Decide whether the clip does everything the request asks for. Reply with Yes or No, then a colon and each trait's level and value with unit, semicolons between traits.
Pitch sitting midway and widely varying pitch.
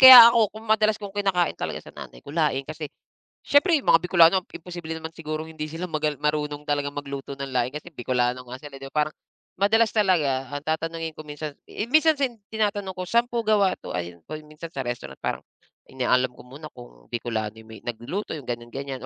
Yes: medium, 155 Hz; wide, 5.9 semitones